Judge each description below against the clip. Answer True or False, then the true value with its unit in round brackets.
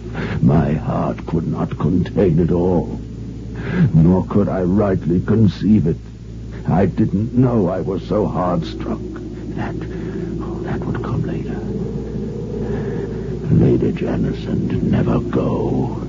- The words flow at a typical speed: False (115 wpm)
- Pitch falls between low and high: False (90 Hz)